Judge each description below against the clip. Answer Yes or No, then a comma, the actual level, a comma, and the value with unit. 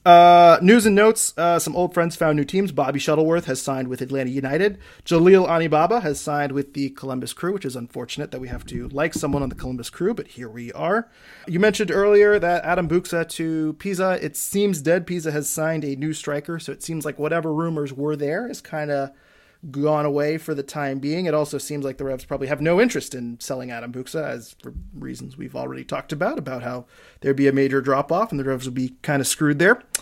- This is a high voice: No, medium, 150 Hz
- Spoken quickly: Yes, fast, 230 wpm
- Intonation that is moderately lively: Yes, average, 3.9 semitones